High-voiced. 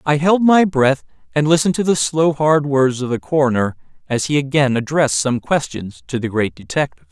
No: medium, 145 Hz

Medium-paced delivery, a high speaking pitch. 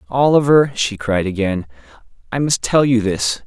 No: average, 155 wpm; low, 115 Hz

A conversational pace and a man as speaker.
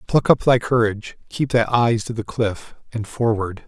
Yes: average, 195 wpm; male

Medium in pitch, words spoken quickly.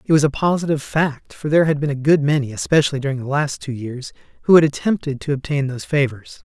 Yes: medium, 145 Hz; fast, 230 wpm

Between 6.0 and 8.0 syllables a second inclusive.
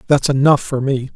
No: 5.3 syllables/s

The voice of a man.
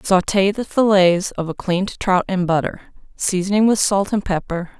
No: female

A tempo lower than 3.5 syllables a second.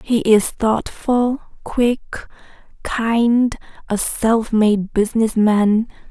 Yes: 2.9 syllables/s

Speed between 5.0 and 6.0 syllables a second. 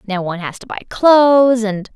Yes: 5.4 syllables/s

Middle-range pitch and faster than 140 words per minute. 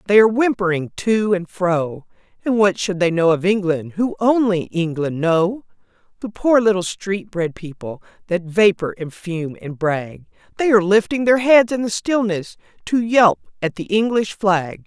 No: high, 195 Hz; average, 175 wpm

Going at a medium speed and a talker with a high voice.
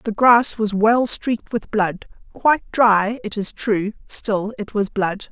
Yes: average, 180 wpm; high, 215 Hz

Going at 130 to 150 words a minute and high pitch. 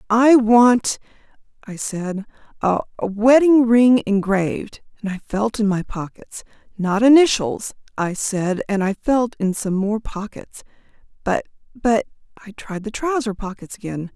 Yes: slow, 135 wpm; high, 215 Hz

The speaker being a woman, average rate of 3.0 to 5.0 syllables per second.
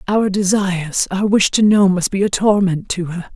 Yes: female; 4.8 syllables/s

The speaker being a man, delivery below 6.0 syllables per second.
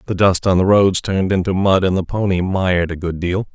Yes: male; 5.7 syllables/s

